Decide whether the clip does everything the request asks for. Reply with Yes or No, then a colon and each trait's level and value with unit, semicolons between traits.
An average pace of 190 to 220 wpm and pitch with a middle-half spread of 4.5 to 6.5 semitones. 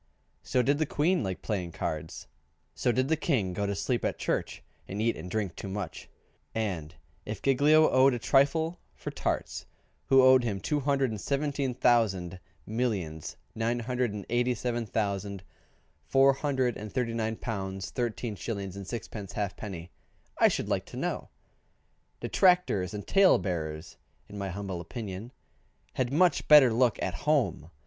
No: average, 160 wpm; average, 5.1 semitones